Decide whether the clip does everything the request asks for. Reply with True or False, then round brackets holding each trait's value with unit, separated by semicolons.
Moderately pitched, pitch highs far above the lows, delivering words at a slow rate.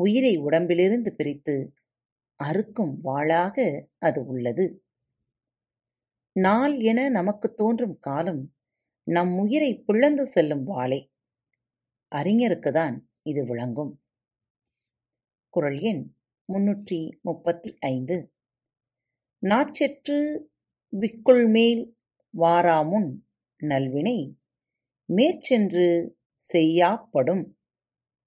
True (170 Hz; 8.8 semitones; 65 wpm)